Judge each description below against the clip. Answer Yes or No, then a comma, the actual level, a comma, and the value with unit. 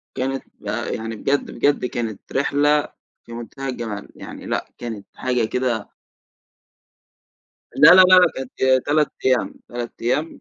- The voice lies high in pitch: No, low, 130 Hz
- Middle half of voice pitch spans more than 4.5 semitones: No, average, 3.4 semitones